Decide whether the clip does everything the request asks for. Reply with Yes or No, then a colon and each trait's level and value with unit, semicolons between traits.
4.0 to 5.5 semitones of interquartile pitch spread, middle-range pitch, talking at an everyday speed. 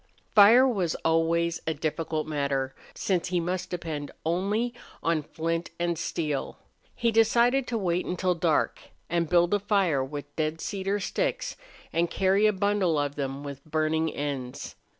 Yes: average, 4.3 semitones; medium, 170 Hz; average, 150 wpm